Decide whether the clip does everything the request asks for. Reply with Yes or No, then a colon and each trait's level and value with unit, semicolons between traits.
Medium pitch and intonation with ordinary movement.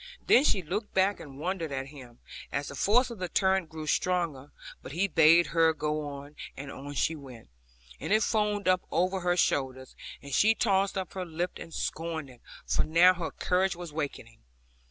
Yes: medium, 165 Hz; average, 4.7 semitones